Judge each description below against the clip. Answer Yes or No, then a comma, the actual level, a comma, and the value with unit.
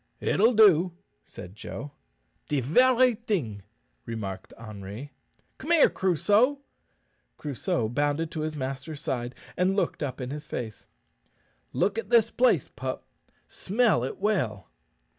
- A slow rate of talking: Yes, slow, 125 wpm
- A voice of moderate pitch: Yes, medium, 150 Hz